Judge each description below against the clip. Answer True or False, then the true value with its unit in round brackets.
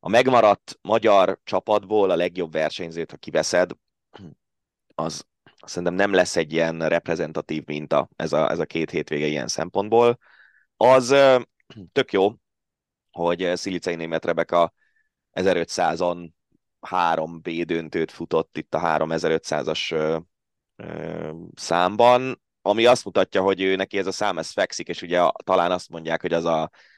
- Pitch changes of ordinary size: True (3.1 semitones)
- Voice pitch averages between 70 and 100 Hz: True (90 Hz)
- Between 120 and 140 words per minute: True (135 wpm)